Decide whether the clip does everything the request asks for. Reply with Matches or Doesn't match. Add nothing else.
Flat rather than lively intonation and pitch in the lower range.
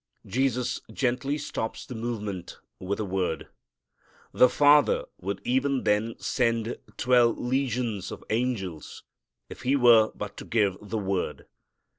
Doesn't match